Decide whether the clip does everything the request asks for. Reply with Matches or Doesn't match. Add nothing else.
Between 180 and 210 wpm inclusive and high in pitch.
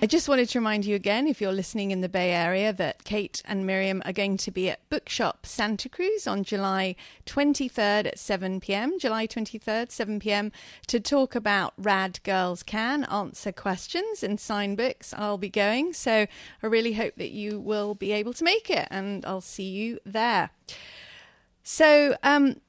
Matches